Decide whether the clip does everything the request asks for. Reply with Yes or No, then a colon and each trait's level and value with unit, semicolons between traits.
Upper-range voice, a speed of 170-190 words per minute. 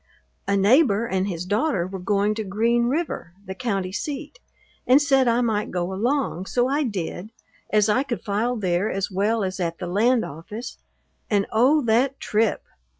Yes: high, 215 Hz; average, 175 wpm